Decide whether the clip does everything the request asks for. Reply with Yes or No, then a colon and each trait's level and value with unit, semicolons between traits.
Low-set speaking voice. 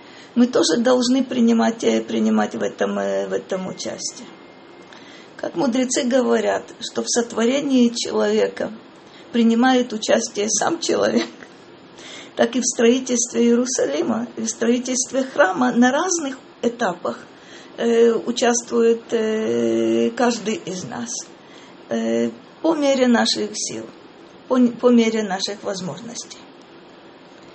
No: high, 235 Hz